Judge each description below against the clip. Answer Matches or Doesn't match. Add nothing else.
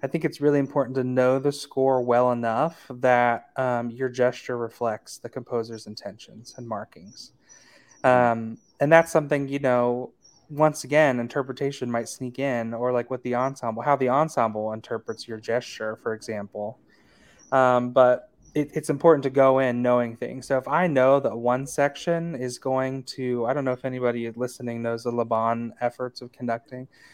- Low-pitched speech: Matches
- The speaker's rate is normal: Matches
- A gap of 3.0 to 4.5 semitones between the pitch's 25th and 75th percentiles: Doesn't match